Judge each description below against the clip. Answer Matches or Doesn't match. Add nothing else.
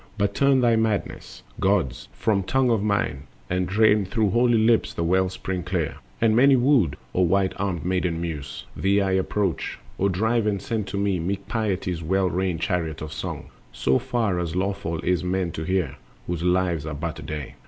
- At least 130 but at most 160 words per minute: Doesn't match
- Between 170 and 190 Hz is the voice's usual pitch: Doesn't match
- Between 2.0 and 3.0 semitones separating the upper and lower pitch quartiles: Doesn't match